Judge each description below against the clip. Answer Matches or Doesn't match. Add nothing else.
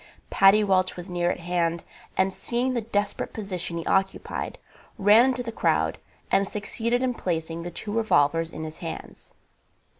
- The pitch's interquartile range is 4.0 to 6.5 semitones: Matches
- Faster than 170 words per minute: Doesn't match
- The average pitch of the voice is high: Matches